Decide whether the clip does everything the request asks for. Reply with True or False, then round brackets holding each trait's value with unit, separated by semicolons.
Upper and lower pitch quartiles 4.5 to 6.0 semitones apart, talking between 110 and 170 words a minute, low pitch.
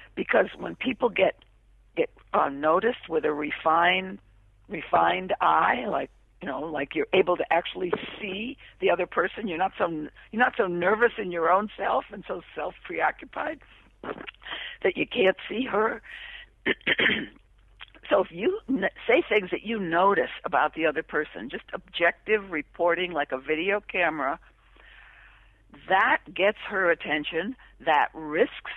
False (5.5 semitones; 140 wpm; 185 Hz)